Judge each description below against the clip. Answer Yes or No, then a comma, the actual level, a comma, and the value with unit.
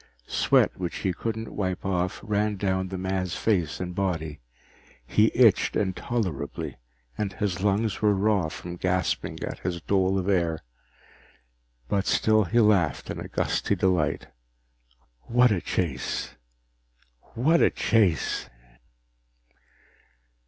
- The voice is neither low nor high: No, very low, 95 Hz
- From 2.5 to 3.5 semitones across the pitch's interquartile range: Yes, average, 3.1 semitones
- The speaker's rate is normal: No, slow, 120 wpm